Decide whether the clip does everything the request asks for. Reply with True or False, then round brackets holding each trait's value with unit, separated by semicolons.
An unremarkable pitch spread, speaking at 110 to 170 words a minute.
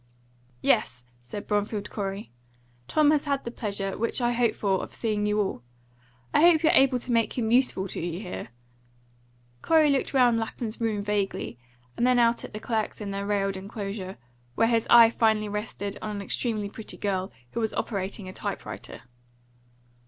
False (3.0 semitones; 180 wpm)